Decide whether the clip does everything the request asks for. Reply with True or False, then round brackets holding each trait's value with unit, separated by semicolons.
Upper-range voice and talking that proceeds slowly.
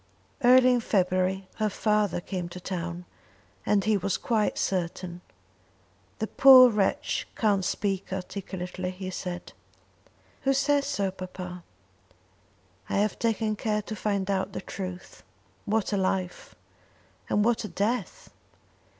True (195 Hz; 130 wpm)